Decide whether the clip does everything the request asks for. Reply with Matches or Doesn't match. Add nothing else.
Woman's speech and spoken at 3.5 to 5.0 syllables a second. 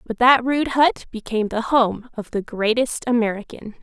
Matches